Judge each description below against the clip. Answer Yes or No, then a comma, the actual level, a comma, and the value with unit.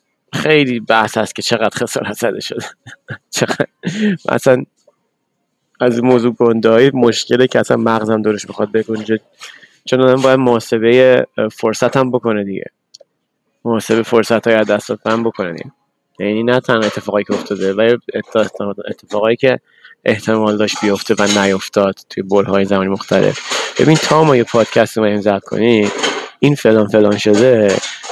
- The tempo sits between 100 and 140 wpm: Yes, average, 135 wpm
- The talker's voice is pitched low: Yes, low, 110 Hz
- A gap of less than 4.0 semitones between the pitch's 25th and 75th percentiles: Yes, average, 2.7 semitones